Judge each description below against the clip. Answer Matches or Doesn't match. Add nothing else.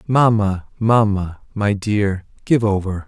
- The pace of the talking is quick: Doesn't match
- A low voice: Matches